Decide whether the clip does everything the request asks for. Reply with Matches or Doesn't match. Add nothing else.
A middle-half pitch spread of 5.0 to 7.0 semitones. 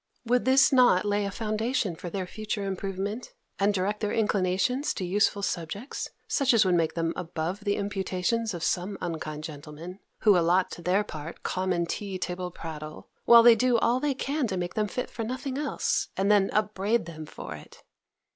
Doesn't match